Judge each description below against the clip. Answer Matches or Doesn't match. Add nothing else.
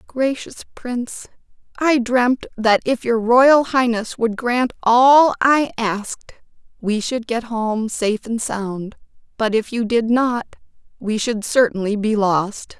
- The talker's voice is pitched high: Matches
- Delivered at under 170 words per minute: Matches